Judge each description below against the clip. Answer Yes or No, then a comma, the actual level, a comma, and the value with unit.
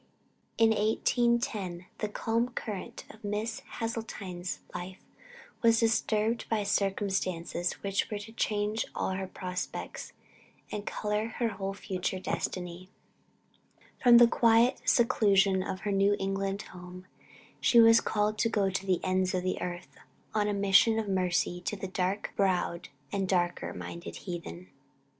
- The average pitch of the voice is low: No, high, 200 Hz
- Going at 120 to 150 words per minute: Yes, average, 145 wpm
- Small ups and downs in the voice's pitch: No, average, 3.1 semitones